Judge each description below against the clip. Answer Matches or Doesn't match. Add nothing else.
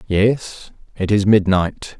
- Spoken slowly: Matches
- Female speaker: Doesn't match